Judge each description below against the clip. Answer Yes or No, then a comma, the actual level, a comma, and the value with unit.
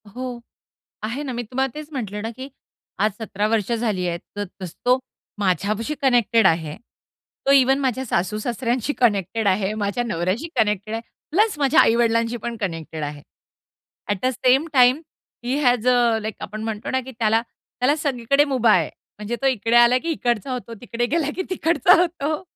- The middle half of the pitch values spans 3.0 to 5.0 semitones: Yes, average, 3.8 semitones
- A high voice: Yes, high, 235 Hz